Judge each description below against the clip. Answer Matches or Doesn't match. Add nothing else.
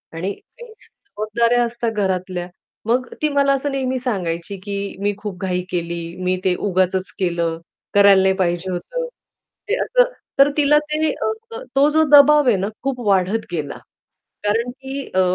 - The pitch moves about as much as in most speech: Doesn't match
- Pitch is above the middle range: Matches